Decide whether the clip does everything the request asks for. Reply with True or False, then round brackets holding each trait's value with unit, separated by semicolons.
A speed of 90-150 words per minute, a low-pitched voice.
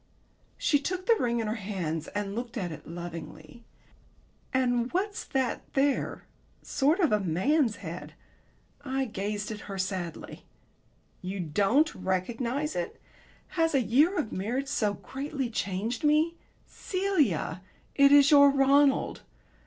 False (135 wpm; 240 Hz)